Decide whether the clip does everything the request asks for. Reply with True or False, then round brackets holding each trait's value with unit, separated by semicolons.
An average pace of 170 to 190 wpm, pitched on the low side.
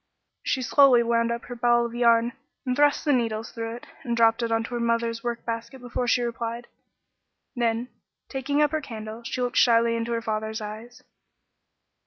False (180 wpm; 235 Hz)